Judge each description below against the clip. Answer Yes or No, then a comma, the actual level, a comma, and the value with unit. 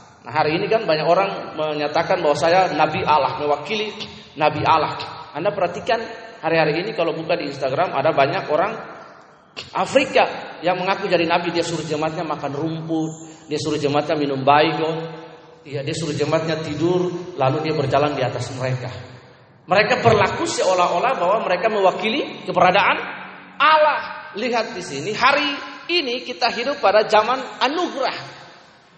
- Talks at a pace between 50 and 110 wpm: No, fast, 140 wpm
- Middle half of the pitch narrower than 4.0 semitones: No, average, 4.5 semitones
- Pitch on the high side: No, medium, 165 Hz